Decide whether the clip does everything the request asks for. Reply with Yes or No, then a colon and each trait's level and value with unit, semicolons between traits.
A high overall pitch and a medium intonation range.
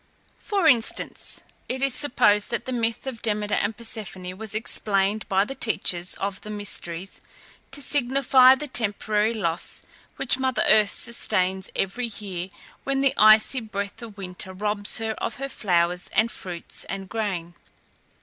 Yes: high, 215 Hz; average, 3.8 semitones